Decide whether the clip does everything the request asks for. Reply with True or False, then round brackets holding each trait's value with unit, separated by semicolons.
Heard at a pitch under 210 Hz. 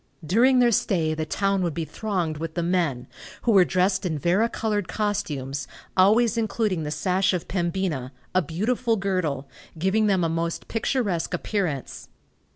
True (185 Hz)